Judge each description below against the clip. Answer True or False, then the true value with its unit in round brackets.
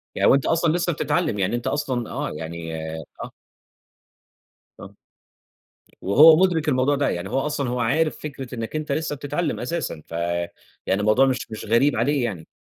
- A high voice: False (135 Hz)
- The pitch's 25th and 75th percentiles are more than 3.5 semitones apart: True (5.3 semitones)